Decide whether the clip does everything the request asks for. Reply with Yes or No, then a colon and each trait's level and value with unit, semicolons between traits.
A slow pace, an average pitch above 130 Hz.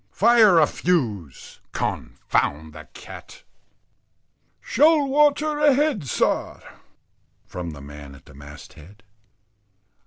Yes: slow, 100 wpm; medium, 140 Hz